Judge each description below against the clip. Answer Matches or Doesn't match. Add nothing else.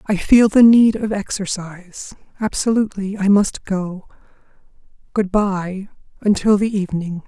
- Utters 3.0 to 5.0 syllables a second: Matches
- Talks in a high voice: Matches